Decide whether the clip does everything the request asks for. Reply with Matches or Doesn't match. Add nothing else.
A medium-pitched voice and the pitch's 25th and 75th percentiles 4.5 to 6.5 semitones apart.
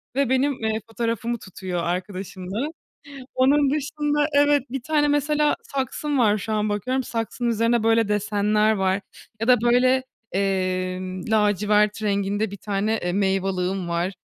Doesn't match